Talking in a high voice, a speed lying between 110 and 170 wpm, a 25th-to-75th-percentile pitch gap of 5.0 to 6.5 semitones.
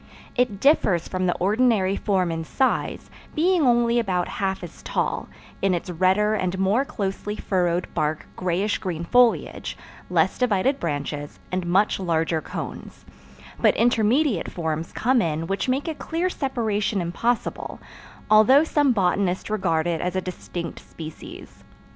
Yes: high, 195 Hz; average, 140 wpm; average, 5.3 semitones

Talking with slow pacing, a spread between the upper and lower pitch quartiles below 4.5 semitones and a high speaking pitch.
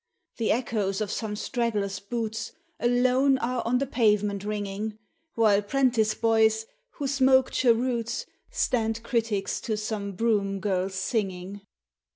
Yes: slow, 125 wpm; average, 3.0 semitones; high, 220 Hz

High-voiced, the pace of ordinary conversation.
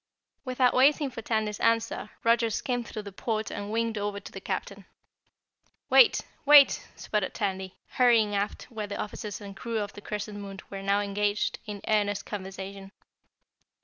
Yes: high, 210 Hz; average, 160 wpm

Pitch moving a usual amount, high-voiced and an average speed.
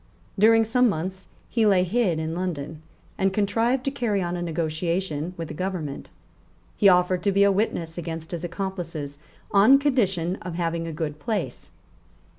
No: average, 3.6 semitones; medium, 180 Hz; average, 165 wpm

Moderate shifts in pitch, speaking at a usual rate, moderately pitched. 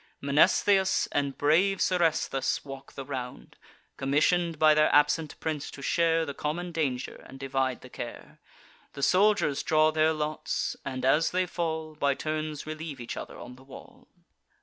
Yes: average, 3.0 semitones; average, 155 wpm; medium, 155 Hz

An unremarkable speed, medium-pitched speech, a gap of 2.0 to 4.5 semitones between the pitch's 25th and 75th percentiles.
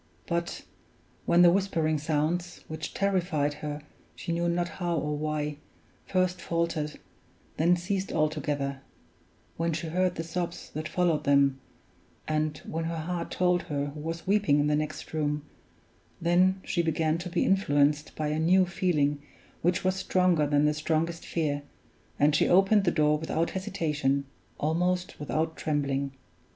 Yes: average, 150 wpm; medium, 160 Hz; average, 2.9 semitones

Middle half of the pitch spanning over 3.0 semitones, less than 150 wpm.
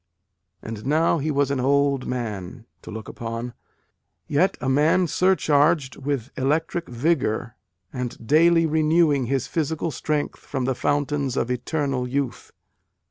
Yes: average, 3.7 semitones; slow, 135 wpm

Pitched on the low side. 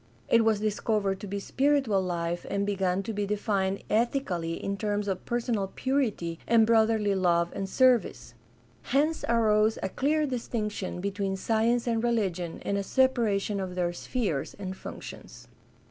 No: high, 205 Hz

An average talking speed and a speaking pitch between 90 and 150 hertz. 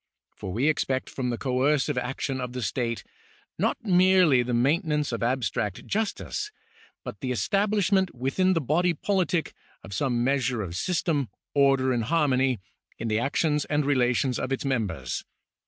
Yes: average, 155 wpm; low, 135 Hz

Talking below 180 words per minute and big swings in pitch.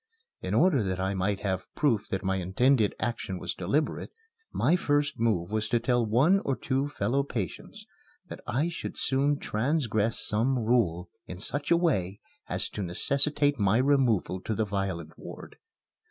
Yes: average, 165 wpm; wide, 6.3 semitones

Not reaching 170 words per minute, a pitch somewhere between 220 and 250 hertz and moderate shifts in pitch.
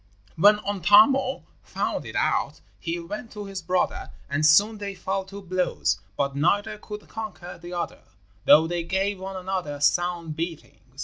No: average, 160 wpm; medium, 185 Hz; average, 3.3 semitones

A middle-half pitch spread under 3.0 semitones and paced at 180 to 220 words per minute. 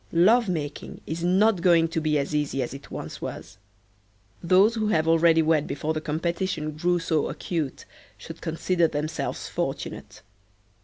No: narrow, 2.5 semitones; average, 155 wpm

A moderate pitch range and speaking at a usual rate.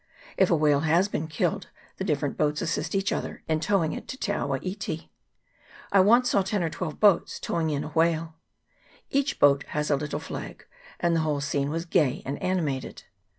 Yes: average, 4.1 semitones; average, 195 wpm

